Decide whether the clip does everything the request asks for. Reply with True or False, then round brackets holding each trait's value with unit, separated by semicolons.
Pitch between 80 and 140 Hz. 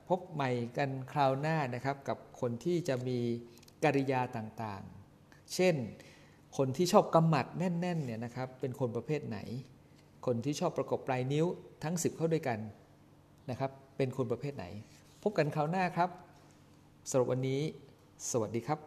True (135 Hz)